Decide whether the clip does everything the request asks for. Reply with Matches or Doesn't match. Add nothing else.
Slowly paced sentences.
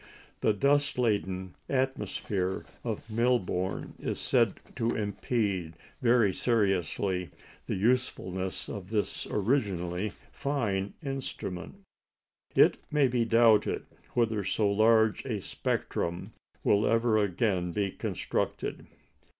Matches